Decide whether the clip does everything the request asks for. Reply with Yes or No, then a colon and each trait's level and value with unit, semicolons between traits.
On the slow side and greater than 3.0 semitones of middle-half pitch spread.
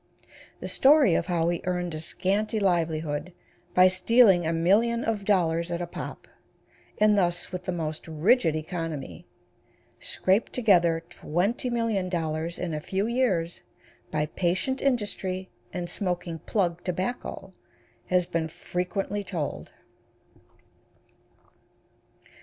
Yes: slow, 115 wpm; average, 3.5 semitones